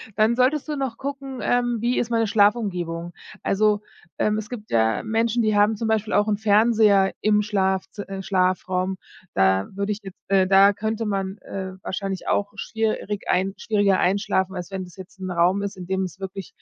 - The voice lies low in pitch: No, high, 200 Hz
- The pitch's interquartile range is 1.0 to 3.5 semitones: Yes, narrow, 2.5 semitones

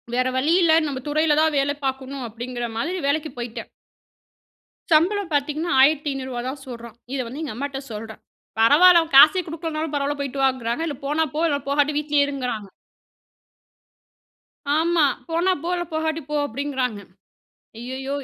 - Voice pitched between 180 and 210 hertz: No, very high, 285 Hz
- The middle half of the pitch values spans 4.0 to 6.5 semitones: No, average, 3.5 semitones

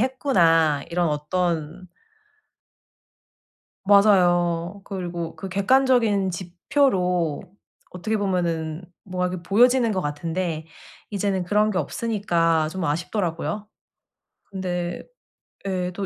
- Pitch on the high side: No, medium, 180 Hz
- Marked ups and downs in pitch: No, average, 3.3 semitones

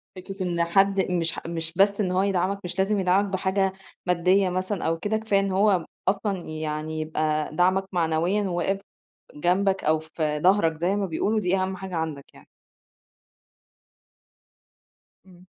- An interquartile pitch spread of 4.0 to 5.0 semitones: No, average, 2.9 semitones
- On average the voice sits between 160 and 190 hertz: Yes, medium, 185 Hz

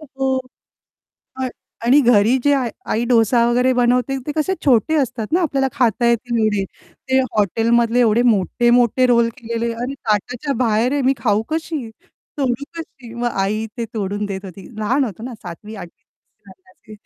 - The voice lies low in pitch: No, high, 235 Hz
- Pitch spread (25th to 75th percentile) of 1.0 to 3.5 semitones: Yes, average, 3.2 semitones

